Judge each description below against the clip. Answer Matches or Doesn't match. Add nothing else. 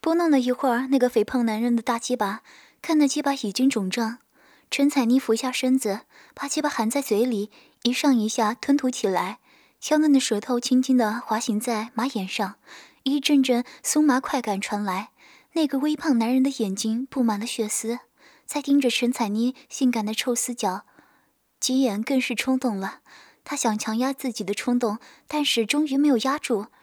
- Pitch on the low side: Doesn't match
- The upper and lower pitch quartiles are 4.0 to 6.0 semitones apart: Doesn't match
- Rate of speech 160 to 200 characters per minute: Doesn't match